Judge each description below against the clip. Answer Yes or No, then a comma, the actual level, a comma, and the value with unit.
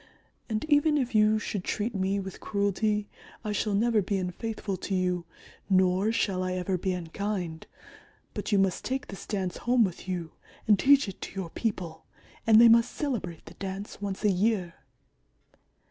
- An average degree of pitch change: Yes, average, 3.0 semitones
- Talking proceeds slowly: No, average, 175 wpm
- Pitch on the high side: Yes, high, 200 Hz